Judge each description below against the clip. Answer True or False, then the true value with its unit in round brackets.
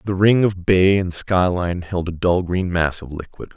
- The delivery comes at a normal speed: False (220 wpm)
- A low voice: True (90 Hz)